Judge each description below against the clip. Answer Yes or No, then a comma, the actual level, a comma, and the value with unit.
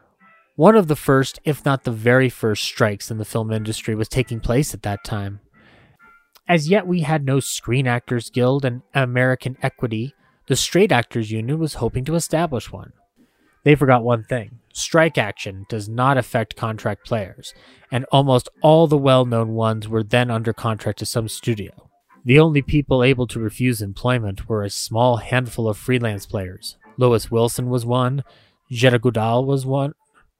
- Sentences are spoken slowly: No, average, 170 wpm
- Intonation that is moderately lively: Yes, average, 3.3 semitones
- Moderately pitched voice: No, low, 125 Hz